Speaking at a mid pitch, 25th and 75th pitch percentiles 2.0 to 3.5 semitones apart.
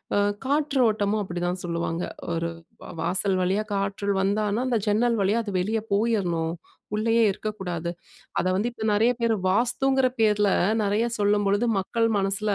No: high, 205 Hz; average, 3.0 semitones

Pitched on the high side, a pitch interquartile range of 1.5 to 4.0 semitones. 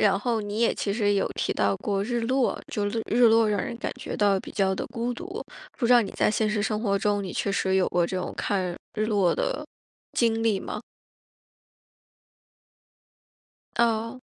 Yes: high, 210 Hz; average, 2.7 semitones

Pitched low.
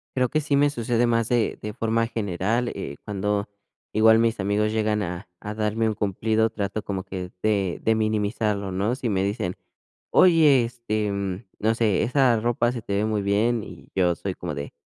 Yes: low, 110 Hz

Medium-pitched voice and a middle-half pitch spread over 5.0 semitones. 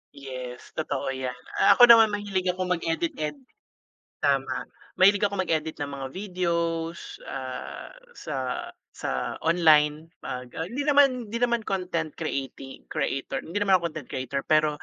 Yes: medium, 165 Hz; wide, 5.6 semitones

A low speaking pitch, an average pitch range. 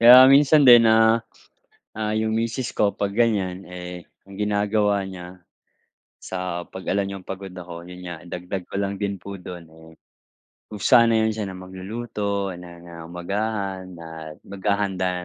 Yes: low, 100 Hz; average, 3.1 semitones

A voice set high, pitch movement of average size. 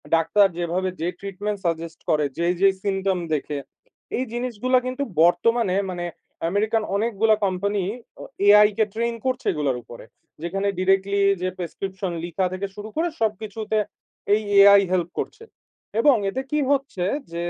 Yes: high, 200 Hz; average, 3.7 semitones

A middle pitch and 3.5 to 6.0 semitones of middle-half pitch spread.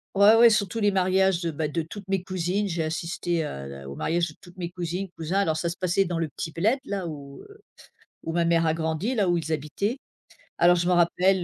No: medium, 175 Hz; average, 2.9 semitones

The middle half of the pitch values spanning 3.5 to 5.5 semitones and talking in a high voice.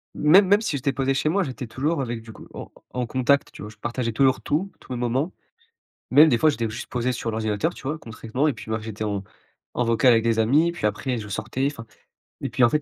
No: average, 4.3 semitones; low, 125 Hz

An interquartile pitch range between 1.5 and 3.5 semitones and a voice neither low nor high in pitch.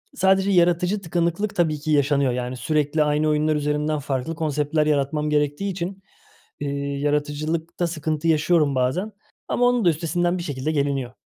Yes: average, 2.9 semitones; medium, 155 Hz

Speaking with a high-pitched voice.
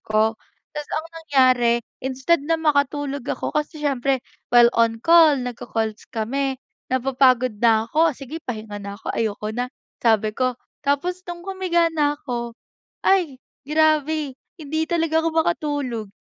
Yes: very high, 275 Hz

